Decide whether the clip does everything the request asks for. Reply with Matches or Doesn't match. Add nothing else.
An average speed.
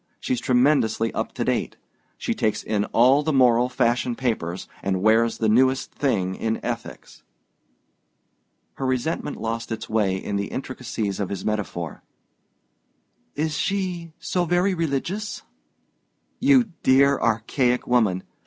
Doesn't match